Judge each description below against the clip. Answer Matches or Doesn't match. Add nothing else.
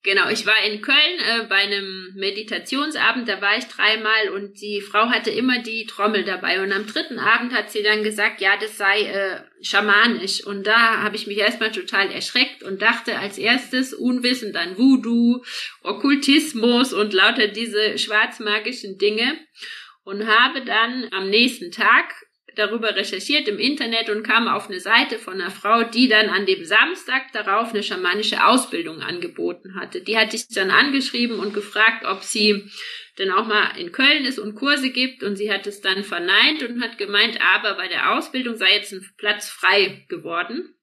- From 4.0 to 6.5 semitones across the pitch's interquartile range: Doesn't match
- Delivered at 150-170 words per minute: Doesn't match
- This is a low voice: Doesn't match